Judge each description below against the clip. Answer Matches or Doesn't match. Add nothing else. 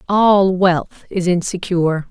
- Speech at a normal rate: Doesn't match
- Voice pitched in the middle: Matches